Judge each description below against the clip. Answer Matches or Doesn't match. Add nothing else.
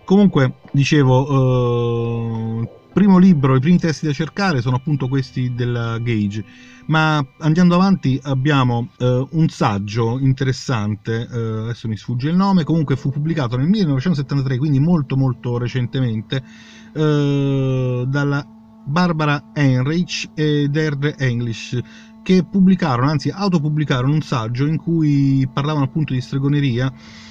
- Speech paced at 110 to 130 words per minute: Matches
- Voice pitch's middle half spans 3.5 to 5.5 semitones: Matches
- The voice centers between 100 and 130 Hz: Doesn't match